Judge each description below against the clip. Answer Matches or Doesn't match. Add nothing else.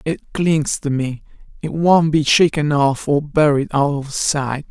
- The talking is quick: Doesn't match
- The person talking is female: Doesn't match